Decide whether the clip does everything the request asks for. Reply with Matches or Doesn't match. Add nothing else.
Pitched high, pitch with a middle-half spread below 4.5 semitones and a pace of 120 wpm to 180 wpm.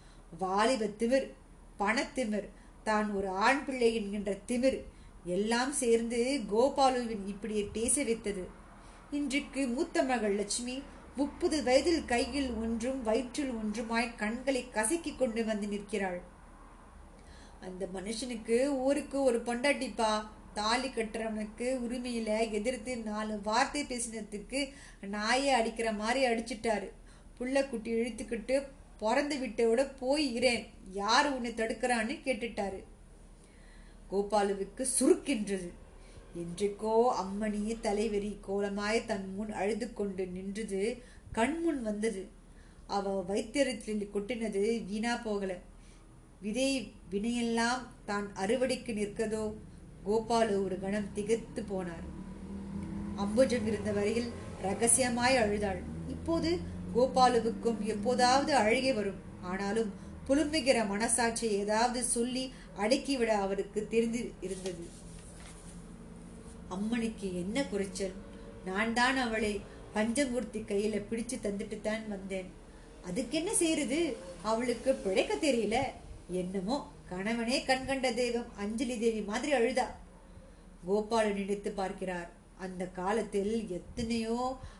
Doesn't match